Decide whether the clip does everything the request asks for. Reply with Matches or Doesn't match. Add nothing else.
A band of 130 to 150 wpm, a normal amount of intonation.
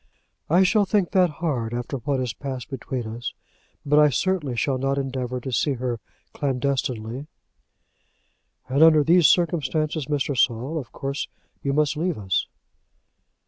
Matches